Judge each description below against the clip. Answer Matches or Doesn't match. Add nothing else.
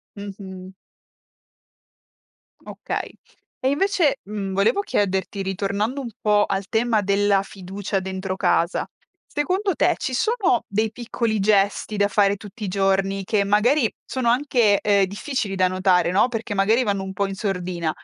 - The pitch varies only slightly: Doesn't match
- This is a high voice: Matches